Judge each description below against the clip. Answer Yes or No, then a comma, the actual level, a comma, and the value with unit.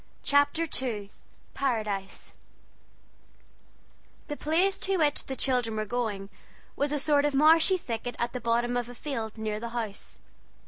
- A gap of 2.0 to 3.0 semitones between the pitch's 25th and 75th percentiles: No, average, 4.8 semitones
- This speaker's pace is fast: No, average, 145 wpm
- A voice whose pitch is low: No, high, 245 Hz